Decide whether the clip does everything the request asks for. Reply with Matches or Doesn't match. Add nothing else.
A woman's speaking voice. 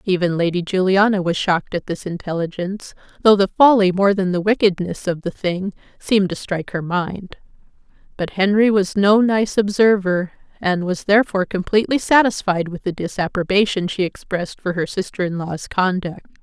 Matches